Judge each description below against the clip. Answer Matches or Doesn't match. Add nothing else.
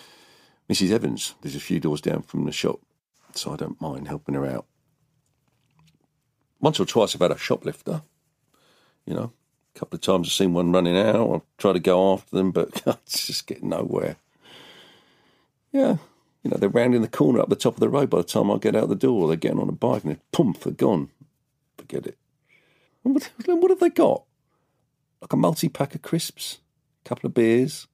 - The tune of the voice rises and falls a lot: Matches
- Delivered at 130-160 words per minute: Doesn't match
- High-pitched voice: Doesn't match